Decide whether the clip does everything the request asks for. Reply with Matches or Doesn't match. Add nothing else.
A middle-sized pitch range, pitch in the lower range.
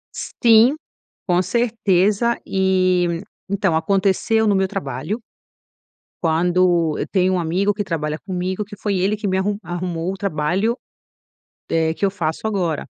Doesn't match